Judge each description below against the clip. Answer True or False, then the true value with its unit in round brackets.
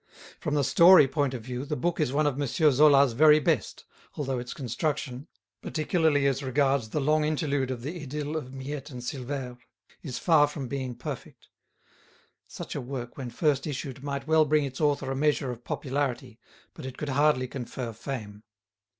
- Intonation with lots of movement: False (2.7 semitones)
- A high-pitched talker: False (140 Hz)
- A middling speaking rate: True (175 wpm)